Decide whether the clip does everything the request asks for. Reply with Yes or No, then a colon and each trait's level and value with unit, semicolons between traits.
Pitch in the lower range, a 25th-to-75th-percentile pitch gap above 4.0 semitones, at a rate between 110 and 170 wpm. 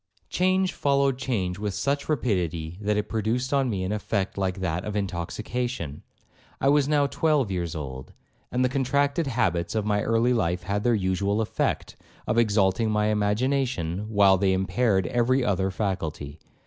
Yes: low, 105 Hz; average, 5.2 semitones; average, 165 wpm